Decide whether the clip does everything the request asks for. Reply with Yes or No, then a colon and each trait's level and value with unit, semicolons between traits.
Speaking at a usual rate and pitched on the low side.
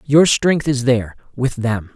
Yes: average, 155 wpm; low, 130 Hz